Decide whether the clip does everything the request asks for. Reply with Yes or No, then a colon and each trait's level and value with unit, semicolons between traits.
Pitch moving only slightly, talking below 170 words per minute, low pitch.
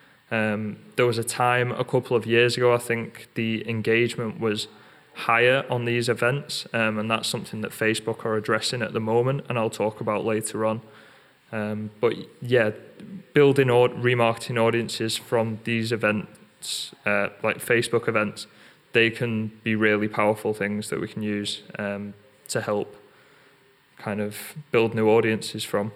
Yes: narrow, 2.0 semitones; average, 155 wpm; low, 115 Hz